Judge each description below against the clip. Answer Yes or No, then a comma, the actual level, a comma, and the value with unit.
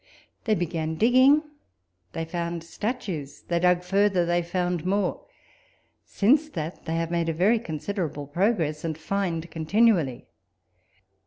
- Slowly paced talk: Yes, slow, 130 wpm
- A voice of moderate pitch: Yes, medium, 175 Hz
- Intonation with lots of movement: No, average, 3.8 semitones